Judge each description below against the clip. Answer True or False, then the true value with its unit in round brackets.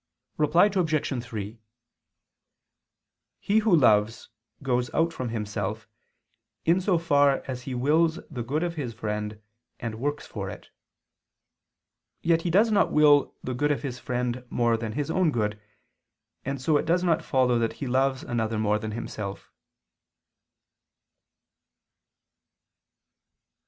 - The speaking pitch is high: False (130 Hz)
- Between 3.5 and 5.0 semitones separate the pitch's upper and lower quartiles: False (5.6 semitones)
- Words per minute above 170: False (135 wpm)